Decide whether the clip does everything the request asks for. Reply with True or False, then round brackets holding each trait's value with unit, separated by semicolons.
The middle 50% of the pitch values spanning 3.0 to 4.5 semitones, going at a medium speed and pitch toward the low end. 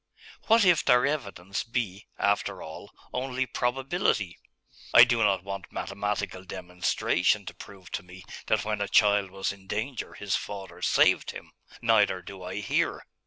True (3.9 semitones; 155 wpm; 100 Hz)